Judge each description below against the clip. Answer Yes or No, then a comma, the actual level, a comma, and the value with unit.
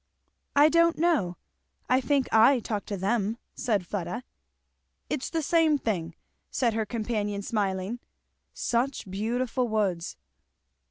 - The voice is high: Yes, high, 225 Hz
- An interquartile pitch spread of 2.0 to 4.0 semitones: No, average, 4.7 semitones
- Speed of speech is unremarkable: No, slow, 120 wpm